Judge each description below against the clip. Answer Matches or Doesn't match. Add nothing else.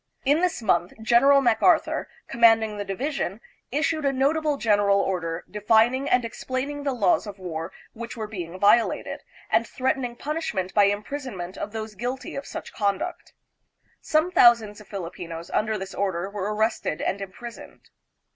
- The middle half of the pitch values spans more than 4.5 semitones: Matches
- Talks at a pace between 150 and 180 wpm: Matches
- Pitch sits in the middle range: Doesn't match